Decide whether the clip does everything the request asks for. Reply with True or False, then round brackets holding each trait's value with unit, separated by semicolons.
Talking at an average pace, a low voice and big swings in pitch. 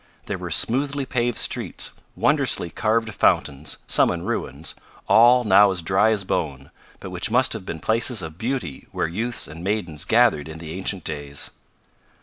True (165 wpm; 95 Hz; 6.5 semitones)